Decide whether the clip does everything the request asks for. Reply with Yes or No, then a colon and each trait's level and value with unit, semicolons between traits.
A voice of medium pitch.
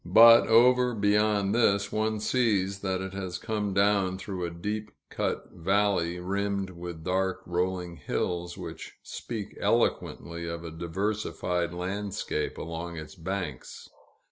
No: very low, 95 Hz